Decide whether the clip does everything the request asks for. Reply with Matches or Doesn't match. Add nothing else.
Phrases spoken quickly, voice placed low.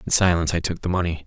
Matches